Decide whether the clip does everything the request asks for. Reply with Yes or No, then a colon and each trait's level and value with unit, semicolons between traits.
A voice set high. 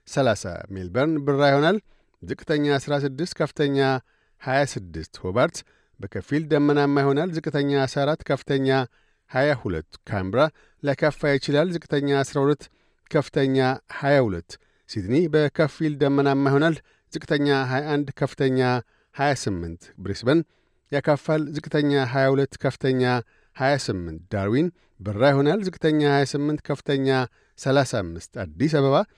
No: medium, 140 Hz